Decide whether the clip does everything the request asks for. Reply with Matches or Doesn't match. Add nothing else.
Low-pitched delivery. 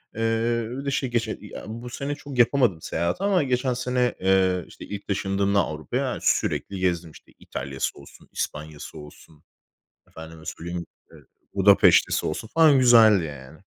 Matches